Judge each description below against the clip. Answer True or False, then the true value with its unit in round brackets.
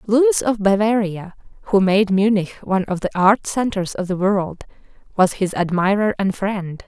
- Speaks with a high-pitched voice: True (200 Hz)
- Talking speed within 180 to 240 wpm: False (165 wpm)